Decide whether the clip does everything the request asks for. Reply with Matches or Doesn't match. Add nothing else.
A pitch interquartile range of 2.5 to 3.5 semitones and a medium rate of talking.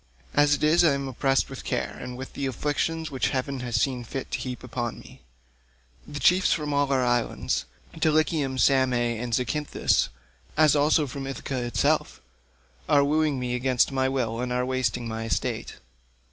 Matches